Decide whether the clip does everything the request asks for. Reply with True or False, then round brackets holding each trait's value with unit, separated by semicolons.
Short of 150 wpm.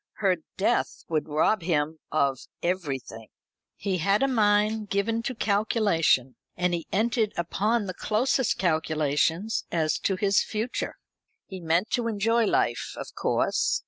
True (140 wpm)